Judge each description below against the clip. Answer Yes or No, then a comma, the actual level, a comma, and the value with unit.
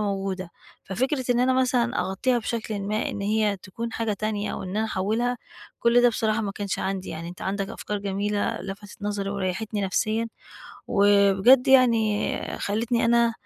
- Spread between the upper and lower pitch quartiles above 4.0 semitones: No, average, 2.9 semitones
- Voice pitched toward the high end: Yes, high, 210 Hz